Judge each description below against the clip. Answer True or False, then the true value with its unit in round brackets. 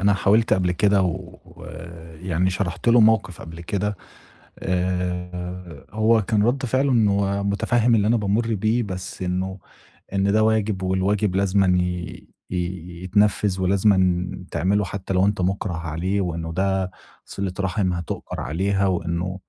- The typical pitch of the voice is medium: False (95 Hz)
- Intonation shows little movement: True (2.3 semitones)